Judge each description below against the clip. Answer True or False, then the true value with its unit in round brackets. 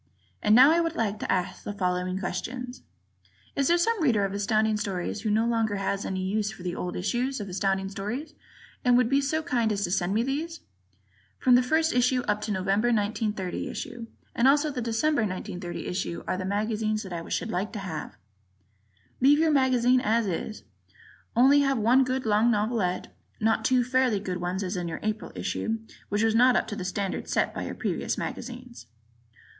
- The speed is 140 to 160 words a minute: False (200 wpm)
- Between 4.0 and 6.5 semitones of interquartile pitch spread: True (4.3 semitones)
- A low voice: False (220 Hz)